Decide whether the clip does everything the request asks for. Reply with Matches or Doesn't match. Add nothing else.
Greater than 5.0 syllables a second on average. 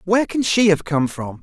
Matches